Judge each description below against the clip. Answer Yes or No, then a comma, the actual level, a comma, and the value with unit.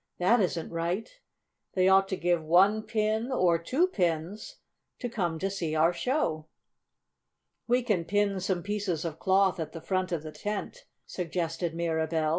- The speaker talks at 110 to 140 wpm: No, average, 165 wpm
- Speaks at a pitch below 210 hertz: Yes, medium, 185 Hz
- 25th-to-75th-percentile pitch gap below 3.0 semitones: No, average, 3.8 semitones